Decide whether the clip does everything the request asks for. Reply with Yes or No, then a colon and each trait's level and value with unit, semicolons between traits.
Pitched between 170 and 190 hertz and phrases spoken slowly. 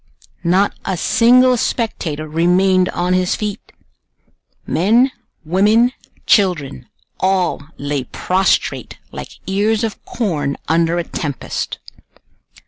Yes: medium, 185 Hz; slow, 100 wpm